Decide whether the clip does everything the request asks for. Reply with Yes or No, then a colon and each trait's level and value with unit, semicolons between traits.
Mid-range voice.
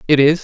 Yes: medium, 150 Hz